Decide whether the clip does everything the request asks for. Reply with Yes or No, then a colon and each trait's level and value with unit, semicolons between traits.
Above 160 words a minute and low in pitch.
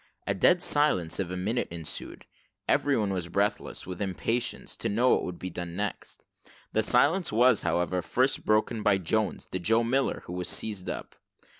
Yes: average, 175 wpm; low, 105 Hz